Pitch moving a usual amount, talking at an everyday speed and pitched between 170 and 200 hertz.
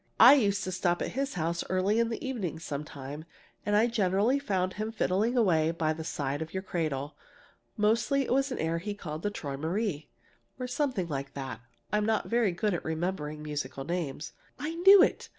No: wide, 6.2 semitones; average, 185 wpm; medium, 185 Hz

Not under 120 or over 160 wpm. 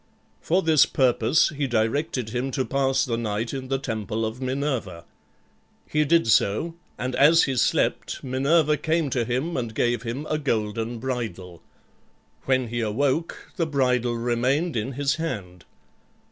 Yes: average, 150 wpm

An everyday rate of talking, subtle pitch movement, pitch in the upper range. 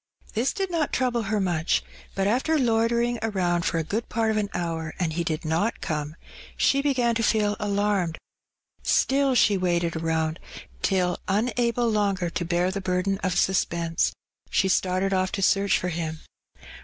No: average, 170 wpm; average, 4.7 semitones; high, 195 Hz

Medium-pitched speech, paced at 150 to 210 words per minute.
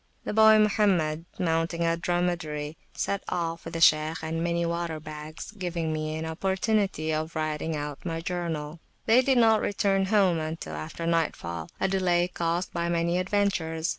Yes: medium, 170 Hz; average, 165 wpm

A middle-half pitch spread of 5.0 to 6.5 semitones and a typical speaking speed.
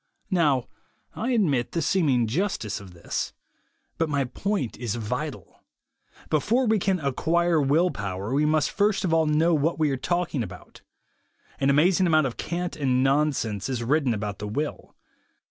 Yes: wide, 5.4 semitones; average, 170 wpm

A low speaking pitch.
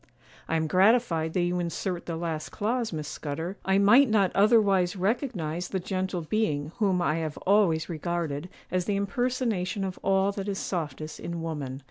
No: medium, 180 Hz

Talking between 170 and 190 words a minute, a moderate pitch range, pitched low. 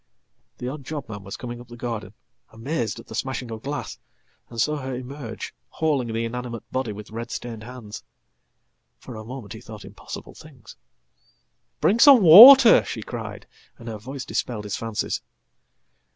No: average, 155 wpm; average, 3.5 semitones; low, 120 Hz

